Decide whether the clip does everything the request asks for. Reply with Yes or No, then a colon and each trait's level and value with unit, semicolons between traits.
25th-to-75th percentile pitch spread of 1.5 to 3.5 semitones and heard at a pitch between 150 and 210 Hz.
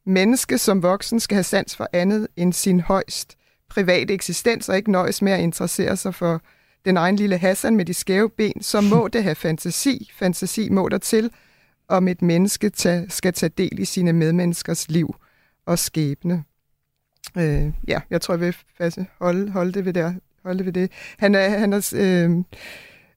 Yes: narrow, 2.6 semitones; medium, 185 Hz